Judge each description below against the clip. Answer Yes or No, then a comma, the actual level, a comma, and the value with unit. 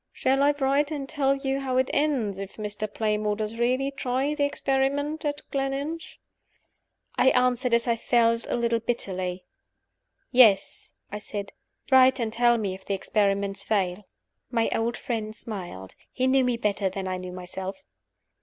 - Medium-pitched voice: No, high, 235 Hz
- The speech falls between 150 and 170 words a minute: Yes, average, 165 wpm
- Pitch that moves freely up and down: No, average, 4.8 semitones